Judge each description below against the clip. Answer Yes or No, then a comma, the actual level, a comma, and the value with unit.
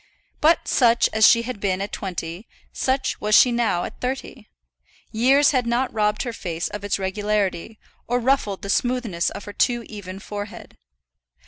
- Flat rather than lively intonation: No, average, 3.7 semitones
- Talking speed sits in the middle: Yes, average, 165 wpm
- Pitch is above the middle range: Yes, high, 220 Hz